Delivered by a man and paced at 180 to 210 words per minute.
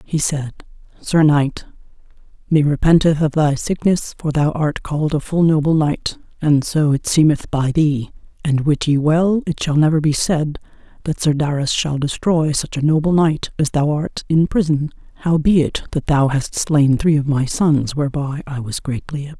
No: female; average, 185 wpm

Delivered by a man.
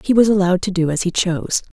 No: female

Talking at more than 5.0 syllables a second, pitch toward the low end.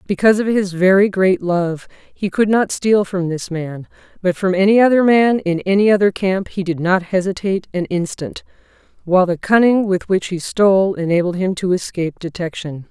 No: 5.2 syllables/s; high, 190 Hz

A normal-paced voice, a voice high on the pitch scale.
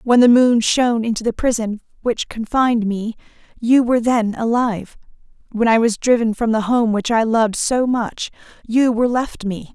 Yes: average, 185 wpm; high, 230 Hz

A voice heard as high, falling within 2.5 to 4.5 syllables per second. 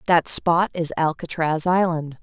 No: medium, 165 Hz; 4.0 syllables/s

